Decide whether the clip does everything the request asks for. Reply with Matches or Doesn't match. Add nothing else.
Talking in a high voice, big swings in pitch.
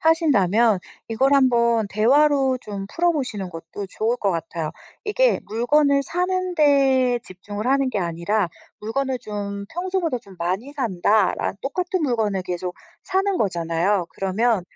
Matches